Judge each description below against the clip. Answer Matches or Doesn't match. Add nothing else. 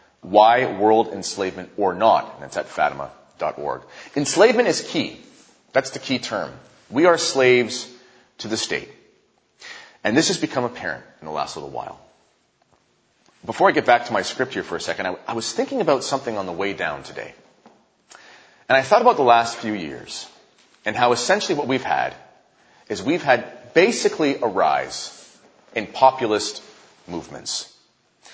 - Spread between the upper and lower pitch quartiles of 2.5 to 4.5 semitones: Matches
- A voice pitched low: Matches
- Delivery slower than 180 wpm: Matches